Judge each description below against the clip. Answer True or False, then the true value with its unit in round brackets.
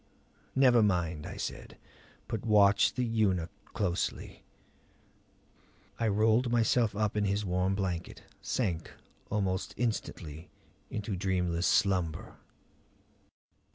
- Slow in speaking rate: True (100 wpm)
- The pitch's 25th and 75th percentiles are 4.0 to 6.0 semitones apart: False (3.5 semitones)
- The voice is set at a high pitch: False (100 Hz)